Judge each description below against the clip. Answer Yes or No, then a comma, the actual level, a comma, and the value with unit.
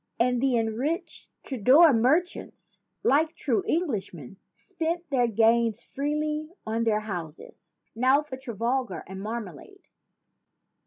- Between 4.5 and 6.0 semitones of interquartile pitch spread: Yes, average, 5.3 semitones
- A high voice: Yes, high, 245 Hz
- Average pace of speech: No, slow, 110 wpm